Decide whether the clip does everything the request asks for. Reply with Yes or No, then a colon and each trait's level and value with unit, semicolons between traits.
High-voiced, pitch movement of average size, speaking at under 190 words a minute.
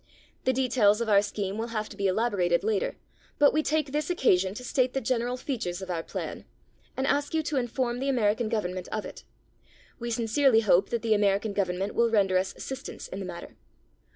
No: high, 225 Hz; average, 4.6 semitones; fast, 205 wpm